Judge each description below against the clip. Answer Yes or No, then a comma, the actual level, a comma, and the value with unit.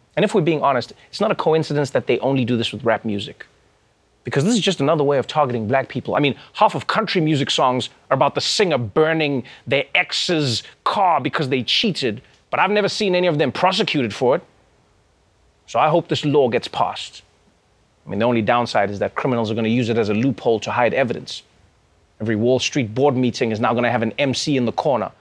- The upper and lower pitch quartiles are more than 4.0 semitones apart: Yes, average, 5.2 semitones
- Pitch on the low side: Yes, low, 130 Hz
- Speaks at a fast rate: Yes, fast, 230 wpm